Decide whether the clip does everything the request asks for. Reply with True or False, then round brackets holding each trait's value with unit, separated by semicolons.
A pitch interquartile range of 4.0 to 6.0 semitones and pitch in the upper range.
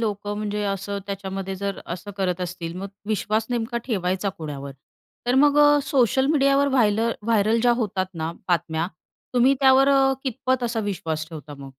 True (5.4 semitones; 205 Hz)